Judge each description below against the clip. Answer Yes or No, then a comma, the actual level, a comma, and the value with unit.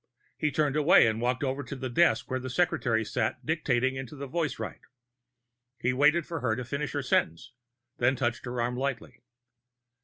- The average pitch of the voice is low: Yes, low, 130 Hz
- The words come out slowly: No, average, 180 wpm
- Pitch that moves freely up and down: No, average, 3.2 semitones